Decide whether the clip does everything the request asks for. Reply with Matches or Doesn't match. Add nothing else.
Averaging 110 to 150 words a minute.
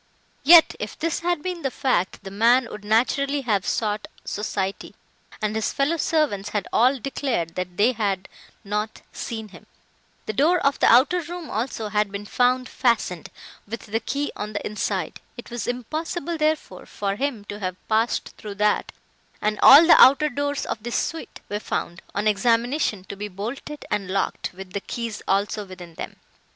Doesn't match